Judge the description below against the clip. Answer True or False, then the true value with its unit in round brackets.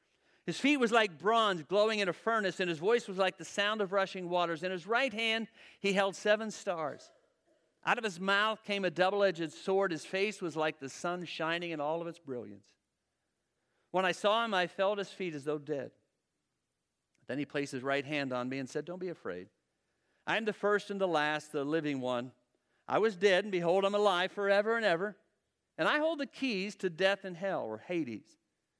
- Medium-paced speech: False (215 wpm)